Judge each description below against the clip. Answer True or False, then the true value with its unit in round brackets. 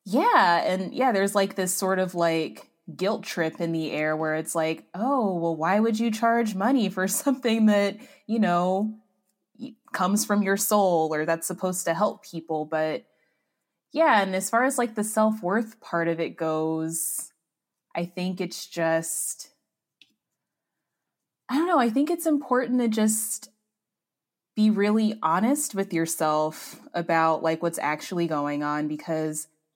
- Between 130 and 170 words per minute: True (155 wpm)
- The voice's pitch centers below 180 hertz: False (190 Hz)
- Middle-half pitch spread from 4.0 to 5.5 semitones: True (5.1 semitones)